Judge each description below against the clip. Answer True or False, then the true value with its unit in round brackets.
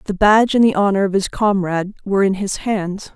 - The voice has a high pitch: True (200 Hz)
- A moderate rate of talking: False (230 wpm)